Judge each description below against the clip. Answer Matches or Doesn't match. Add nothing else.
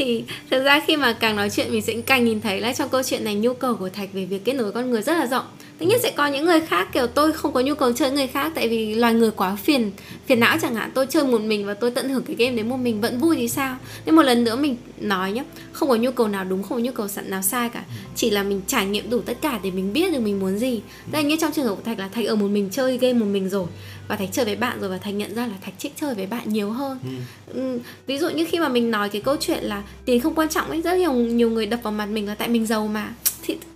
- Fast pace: Matches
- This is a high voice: Matches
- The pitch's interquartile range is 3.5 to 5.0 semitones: Matches